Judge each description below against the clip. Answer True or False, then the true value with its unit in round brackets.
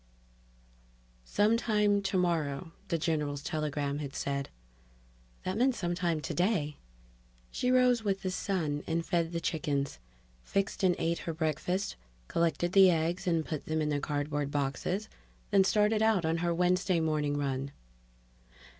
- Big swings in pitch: False (4.3 semitones)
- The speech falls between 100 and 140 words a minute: True (135 wpm)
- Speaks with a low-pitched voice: False (165 Hz)